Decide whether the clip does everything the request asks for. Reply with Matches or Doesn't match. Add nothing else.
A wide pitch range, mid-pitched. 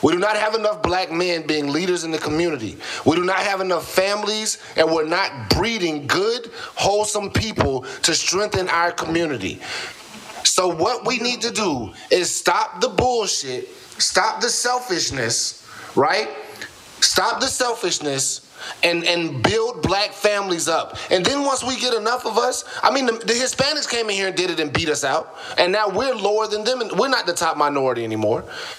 Doesn't match